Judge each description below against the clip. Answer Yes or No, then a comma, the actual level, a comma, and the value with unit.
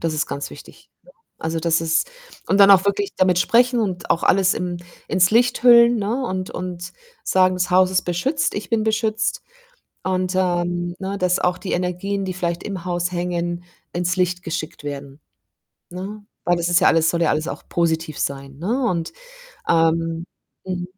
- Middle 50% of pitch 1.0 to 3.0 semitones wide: Yes, narrow, 2.5 semitones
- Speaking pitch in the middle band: Yes, medium, 180 Hz